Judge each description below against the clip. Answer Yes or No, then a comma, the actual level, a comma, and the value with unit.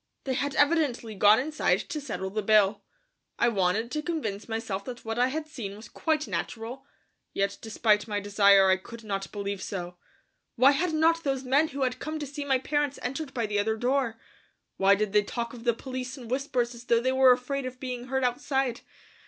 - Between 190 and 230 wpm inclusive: Yes, fast, 205 wpm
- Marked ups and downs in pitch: No, average, 4.4 semitones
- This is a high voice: Yes, high, 245 Hz